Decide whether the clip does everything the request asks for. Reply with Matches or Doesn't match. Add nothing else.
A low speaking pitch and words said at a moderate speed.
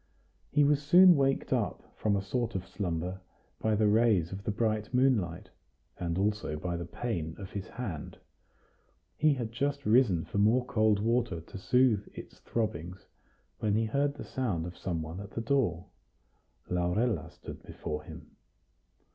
Matches